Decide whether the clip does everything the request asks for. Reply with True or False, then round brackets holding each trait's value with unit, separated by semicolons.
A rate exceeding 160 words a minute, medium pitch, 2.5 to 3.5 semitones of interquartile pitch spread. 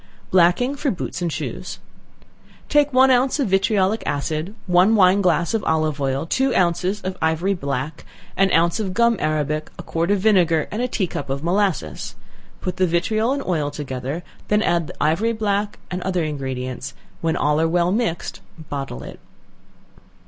False (170 wpm; 175 Hz; 5.1 semitones)